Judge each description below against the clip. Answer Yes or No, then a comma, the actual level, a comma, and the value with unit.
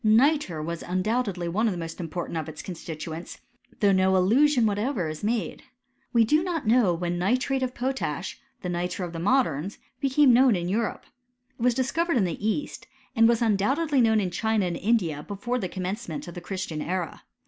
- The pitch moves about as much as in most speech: No, wide, 6.0 semitones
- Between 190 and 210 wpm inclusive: Yes, average, 195 wpm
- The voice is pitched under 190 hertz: No, high, 205 Hz